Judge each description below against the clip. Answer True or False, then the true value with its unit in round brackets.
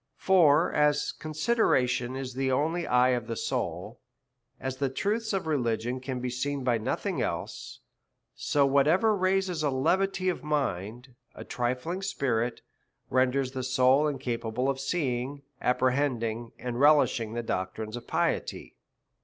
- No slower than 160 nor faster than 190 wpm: False (145 wpm)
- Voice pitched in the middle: False (130 Hz)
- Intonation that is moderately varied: True (3.6 semitones)